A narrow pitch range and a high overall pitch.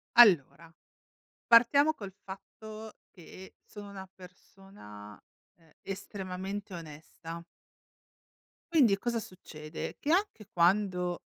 No: average, 4.1 semitones; high, 195 Hz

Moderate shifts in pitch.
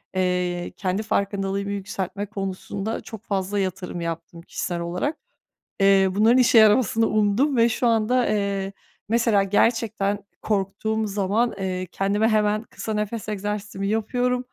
No: narrow, 2.3 semitones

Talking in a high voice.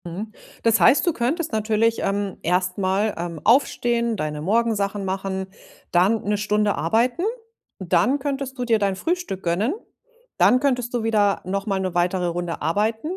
Yes: high, 210 Hz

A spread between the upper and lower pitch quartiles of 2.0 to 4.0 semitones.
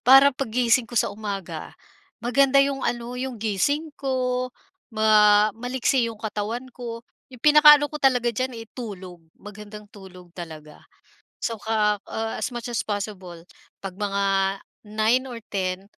Yes: average, 3.6 semitones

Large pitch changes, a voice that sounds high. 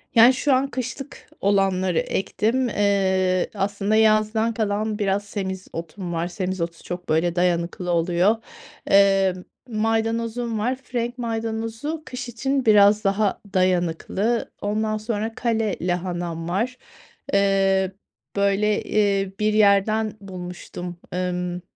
No: average, 3.3 semitones; high, 200 Hz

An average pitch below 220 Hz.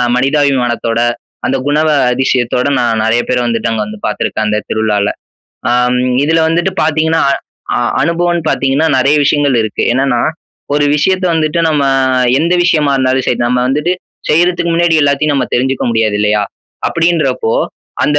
Yes: low, 135 Hz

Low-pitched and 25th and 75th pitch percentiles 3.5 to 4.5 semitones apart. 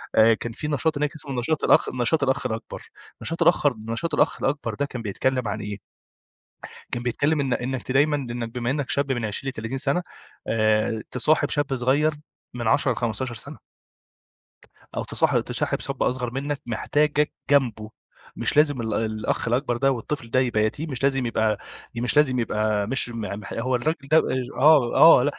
Yes: low, 125 Hz; average, 3.8 semitones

